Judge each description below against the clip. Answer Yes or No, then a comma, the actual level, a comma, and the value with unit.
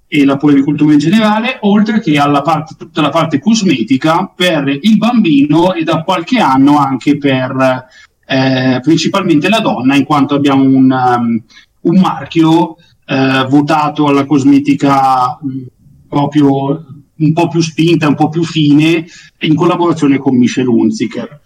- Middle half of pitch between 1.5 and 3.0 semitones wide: No, average, 3.4 semitones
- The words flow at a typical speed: Yes, average, 135 wpm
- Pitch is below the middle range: No, medium, 150 Hz